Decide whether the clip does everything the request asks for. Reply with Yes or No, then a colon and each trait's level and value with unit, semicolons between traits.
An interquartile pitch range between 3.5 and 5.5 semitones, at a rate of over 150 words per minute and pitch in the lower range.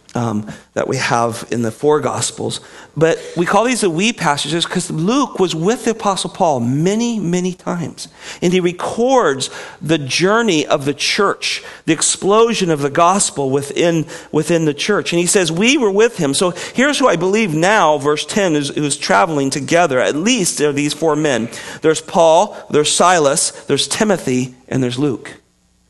No: average, 5.1 semitones; average, 180 wpm; medium, 165 Hz